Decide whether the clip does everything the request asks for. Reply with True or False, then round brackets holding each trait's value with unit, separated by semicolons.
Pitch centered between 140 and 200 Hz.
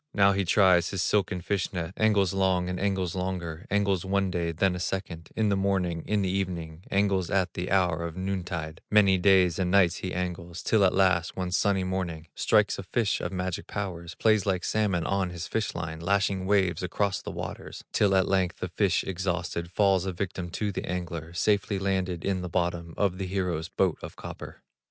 False (95 Hz)